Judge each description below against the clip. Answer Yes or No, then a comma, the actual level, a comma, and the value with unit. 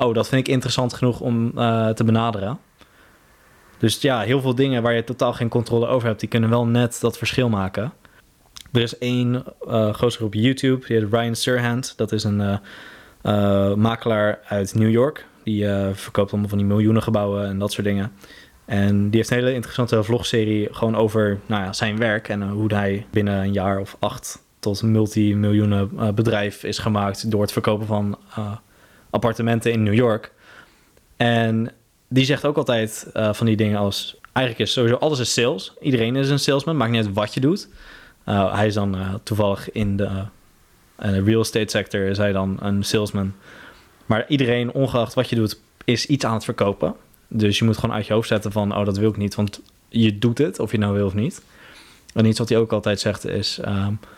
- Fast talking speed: Yes, fast, 205 wpm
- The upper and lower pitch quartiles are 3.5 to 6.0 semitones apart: No, narrow, 2.5 semitones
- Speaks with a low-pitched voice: Yes, low, 110 Hz